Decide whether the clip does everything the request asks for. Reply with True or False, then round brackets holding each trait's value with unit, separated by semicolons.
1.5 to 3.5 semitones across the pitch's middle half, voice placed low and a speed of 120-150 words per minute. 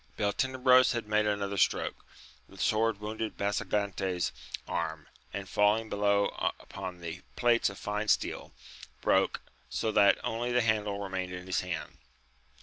True (2.4 semitones; 105 Hz; 145 wpm)